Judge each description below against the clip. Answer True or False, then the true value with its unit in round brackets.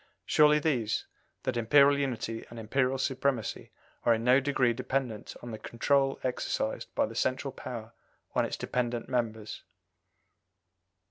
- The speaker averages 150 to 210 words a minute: False (135 wpm)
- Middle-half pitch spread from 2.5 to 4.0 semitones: True (2.9 semitones)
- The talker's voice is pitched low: True (125 Hz)